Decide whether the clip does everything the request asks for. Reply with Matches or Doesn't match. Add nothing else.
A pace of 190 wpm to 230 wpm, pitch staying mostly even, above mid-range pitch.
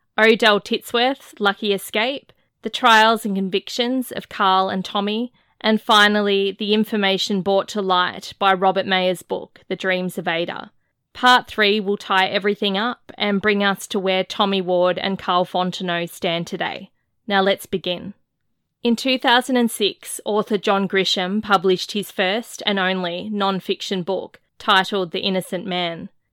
Doesn't match